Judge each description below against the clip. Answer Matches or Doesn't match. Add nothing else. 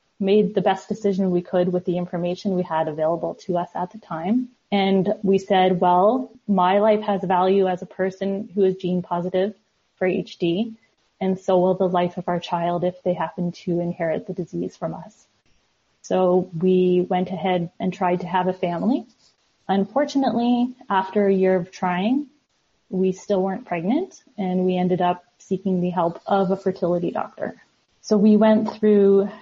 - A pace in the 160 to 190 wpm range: Matches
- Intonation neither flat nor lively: Doesn't match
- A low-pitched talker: Doesn't match